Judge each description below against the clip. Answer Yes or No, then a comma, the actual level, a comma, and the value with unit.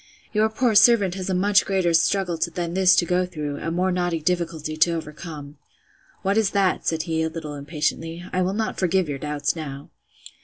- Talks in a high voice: No, medium, 175 Hz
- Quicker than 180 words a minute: Yes, average, 195 wpm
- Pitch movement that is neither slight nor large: Yes, average, 3.3 semitones